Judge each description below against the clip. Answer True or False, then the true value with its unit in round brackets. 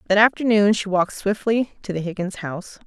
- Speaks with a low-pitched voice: False (200 Hz)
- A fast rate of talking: False (190 wpm)